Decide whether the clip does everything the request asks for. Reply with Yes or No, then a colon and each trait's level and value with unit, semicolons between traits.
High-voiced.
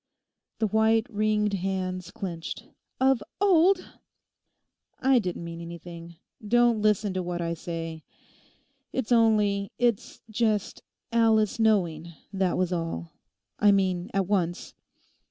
Yes: high, 200 Hz